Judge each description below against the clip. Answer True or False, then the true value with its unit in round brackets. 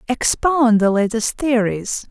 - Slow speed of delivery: True (115 wpm)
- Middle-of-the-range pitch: False (235 Hz)